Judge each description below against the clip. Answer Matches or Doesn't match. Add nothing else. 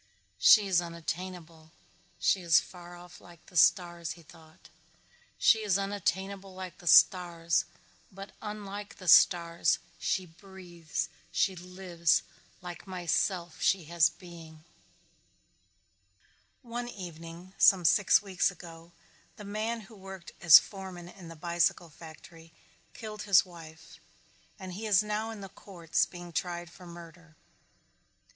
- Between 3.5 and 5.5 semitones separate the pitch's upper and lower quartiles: Doesn't match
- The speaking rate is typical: Doesn't match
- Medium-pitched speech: Matches